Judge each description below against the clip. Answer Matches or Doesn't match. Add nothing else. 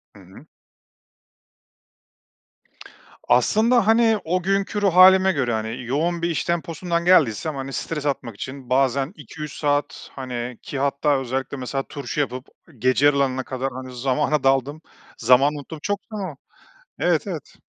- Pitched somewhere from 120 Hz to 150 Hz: Matches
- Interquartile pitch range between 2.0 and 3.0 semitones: Doesn't match